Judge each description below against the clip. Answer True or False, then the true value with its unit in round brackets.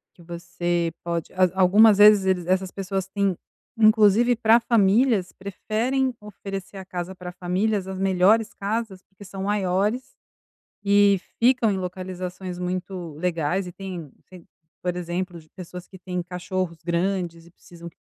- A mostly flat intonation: True (2.3 semitones)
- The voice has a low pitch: False (190 Hz)